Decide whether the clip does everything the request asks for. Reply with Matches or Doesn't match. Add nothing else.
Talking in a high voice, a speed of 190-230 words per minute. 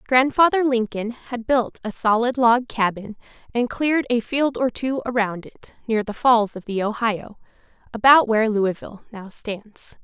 Doesn't match